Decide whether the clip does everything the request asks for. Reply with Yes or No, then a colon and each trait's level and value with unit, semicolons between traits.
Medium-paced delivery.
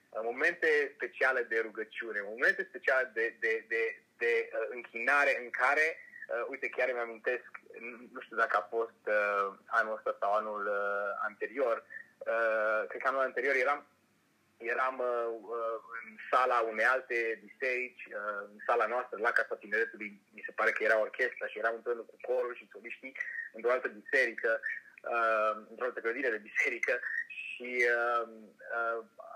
Yes: average, 155 wpm